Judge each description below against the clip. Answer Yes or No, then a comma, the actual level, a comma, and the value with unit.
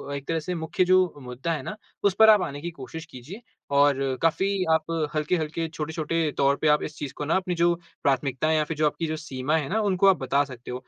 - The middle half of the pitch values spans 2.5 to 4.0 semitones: Yes, average, 3.3 semitones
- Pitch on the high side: No, medium, 155 Hz